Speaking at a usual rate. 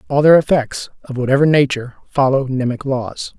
Yes: average, 160 wpm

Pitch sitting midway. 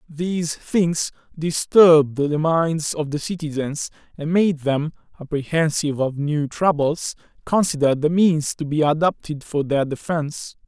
Yes: medium, 155 Hz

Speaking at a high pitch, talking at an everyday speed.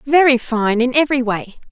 Yes: very high, 250 Hz; average, 175 wpm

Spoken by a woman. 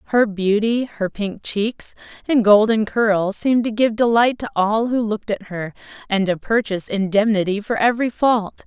Yes: female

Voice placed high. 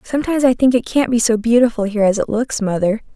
Yes: high, 230 Hz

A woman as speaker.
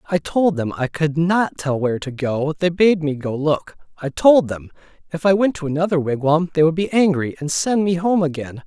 No: male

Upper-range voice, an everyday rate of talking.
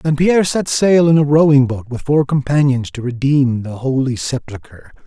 No: low, 135 Hz; average, 190 wpm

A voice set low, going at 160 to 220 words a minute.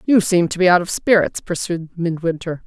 No: medium, 175 Hz; average, 200 wpm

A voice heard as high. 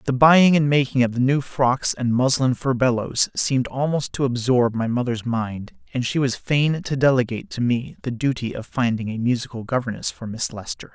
No: low, 125 Hz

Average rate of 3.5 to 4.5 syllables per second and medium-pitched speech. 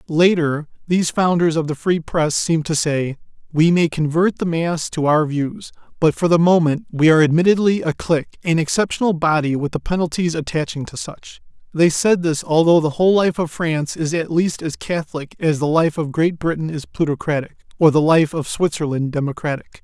No: 5.4 syllables/s; medium, 160 Hz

